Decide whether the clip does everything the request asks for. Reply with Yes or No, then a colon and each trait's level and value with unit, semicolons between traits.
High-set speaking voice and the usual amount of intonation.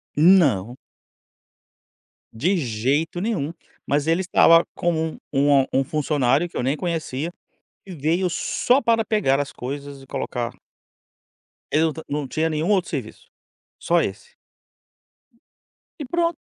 No: medium, 155 Hz; average, 4.7 semitones